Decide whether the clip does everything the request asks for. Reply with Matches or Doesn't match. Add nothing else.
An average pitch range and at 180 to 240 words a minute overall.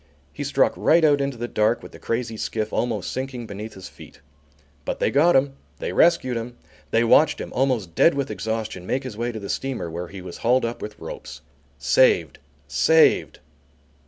Matches